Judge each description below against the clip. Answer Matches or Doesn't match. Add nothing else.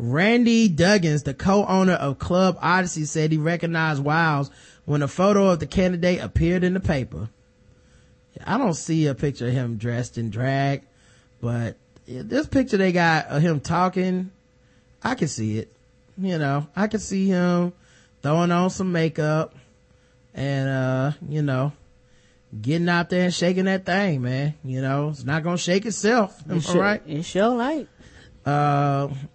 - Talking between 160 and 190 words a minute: Matches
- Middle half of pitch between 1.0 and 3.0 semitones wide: Doesn't match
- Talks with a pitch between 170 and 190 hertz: Doesn't match